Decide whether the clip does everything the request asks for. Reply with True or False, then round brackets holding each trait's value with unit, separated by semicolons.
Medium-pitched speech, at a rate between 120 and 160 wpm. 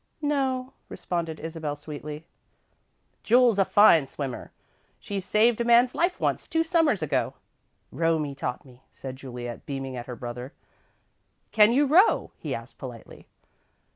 True (165 Hz; 140 wpm)